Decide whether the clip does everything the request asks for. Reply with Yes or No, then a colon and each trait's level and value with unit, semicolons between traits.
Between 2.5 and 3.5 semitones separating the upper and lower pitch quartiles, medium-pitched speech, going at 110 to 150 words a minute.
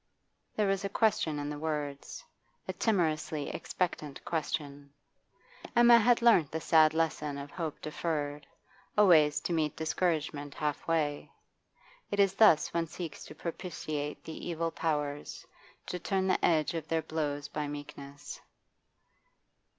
Yes: average, 2.9 semitones; medium, 155 Hz; slow, 135 wpm